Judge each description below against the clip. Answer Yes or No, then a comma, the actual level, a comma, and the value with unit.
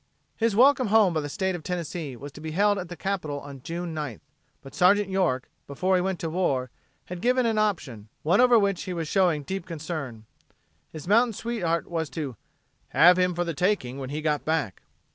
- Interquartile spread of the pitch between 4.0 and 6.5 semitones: Yes, average, 4.7 semitones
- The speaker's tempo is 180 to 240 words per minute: Yes, fast, 205 wpm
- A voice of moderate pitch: Yes, medium, 175 Hz